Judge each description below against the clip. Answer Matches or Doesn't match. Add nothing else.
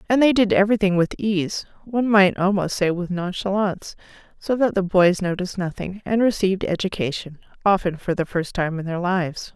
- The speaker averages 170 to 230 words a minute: Matches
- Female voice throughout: Matches